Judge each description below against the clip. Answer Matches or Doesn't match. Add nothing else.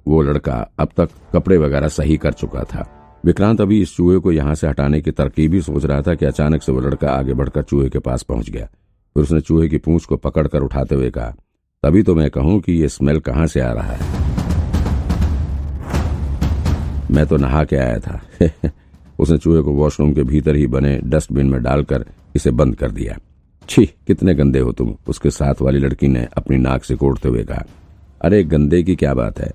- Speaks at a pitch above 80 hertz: Doesn't match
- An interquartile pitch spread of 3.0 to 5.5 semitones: Doesn't match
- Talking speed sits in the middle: Doesn't match